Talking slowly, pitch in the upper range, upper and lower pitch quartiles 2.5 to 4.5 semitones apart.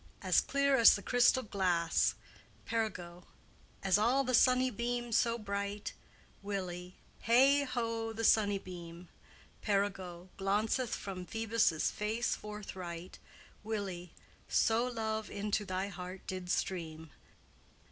Yes: slow, 110 wpm; high, 210 Hz; average, 3.9 semitones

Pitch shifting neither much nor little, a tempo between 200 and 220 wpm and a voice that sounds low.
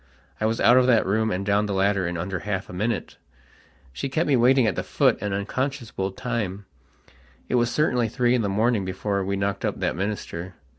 Yes: average, 3.6 semitones; fast, 205 wpm; low, 105 Hz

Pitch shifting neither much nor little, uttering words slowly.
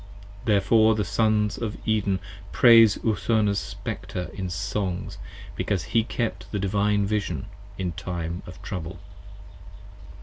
Yes: average, 3.0 semitones; slow, 125 wpm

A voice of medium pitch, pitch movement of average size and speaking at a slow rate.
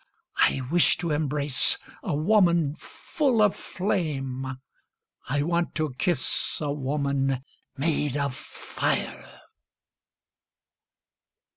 Yes: medium, 150 Hz; average, 3.6 semitones; slow, 95 wpm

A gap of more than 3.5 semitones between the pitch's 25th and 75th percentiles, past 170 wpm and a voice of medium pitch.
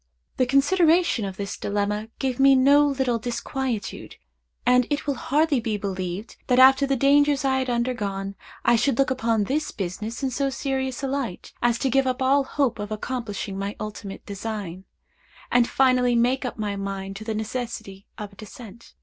No: average, 4.4 semitones; average, 180 wpm; high, 240 Hz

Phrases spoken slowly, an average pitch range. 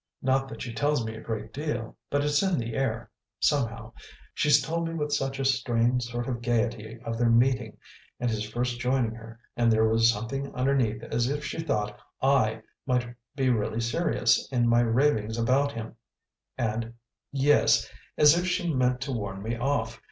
No: average, 180 wpm; average, 3.3 semitones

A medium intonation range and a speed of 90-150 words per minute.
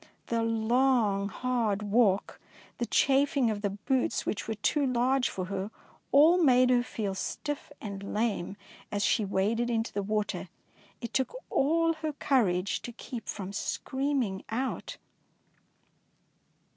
Yes: average, 4.5 semitones; average, 145 wpm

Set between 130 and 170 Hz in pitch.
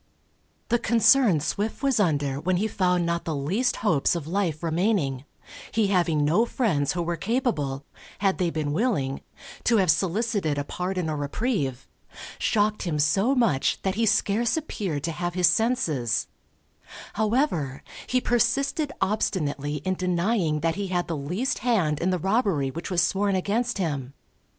No: medium, 180 Hz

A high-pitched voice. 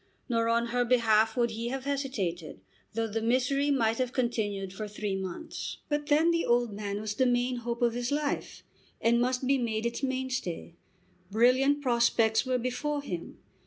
Yes: high, 240 Hz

